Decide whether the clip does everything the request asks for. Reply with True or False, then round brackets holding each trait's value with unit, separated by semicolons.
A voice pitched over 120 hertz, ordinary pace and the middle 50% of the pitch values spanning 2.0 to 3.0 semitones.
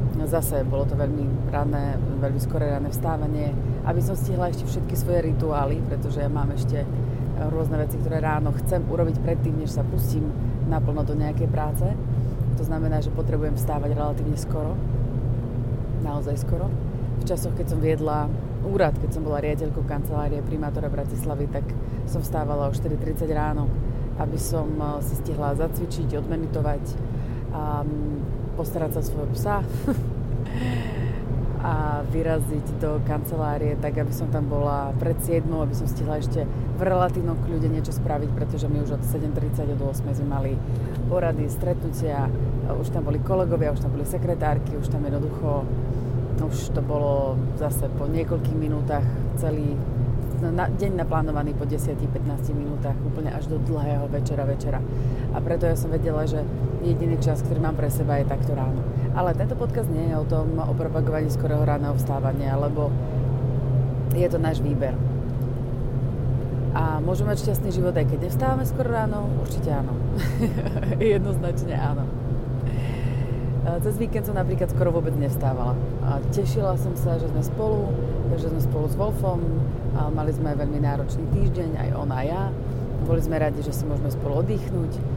True (130 Hz; 155 wpm; 2.5 semitones)